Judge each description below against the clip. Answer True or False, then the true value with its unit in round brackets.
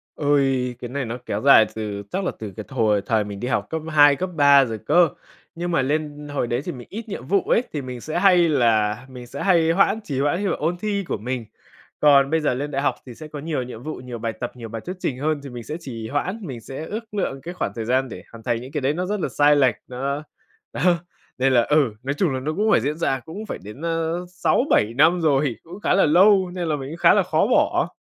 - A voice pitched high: False (140 Hz)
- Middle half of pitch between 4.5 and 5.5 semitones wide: True (5.1 semitones)